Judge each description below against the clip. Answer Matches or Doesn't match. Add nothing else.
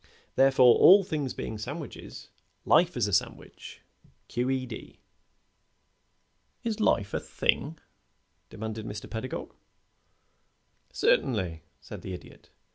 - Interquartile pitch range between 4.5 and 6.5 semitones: Matches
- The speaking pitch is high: Doesn't match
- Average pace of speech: Doesn't match